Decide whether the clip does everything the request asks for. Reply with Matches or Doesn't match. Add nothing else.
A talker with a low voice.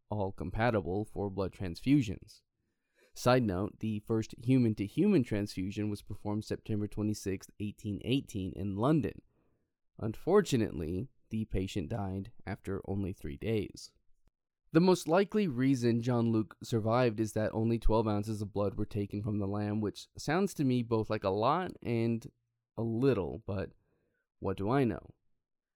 Matches